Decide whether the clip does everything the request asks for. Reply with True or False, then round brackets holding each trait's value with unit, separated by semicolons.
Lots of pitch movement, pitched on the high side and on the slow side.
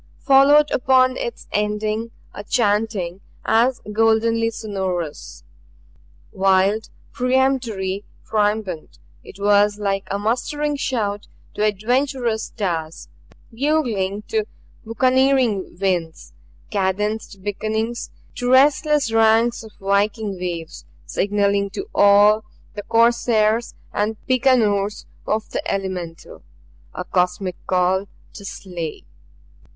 False (3.3 semitones; 210 Hz; 95 wpm)